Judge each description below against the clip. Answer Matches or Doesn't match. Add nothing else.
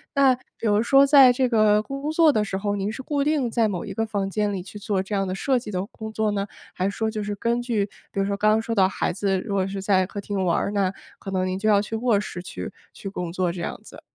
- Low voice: Doesn't match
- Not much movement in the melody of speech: Doesn't match